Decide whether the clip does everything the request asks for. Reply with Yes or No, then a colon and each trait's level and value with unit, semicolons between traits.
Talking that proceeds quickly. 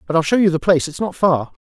Yes: fast, 330 wpm